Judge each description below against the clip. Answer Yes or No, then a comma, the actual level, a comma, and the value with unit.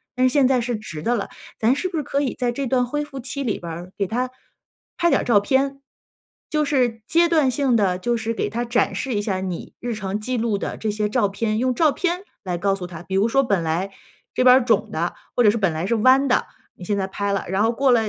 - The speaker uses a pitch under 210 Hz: No, high, 230 Hz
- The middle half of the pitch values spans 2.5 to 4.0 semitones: No, average, 4.6 semitones